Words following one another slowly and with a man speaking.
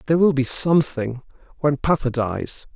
Yes: slow, 130 wpm; male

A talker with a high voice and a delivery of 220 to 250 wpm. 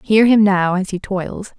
Yes: high, 200 Hz; fast, 225 wpm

